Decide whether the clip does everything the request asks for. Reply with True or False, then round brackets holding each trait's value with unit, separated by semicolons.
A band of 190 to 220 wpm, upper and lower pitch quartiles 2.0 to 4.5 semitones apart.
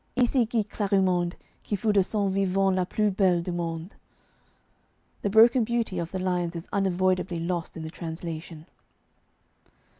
False (150 wpm; 2.9 semitones)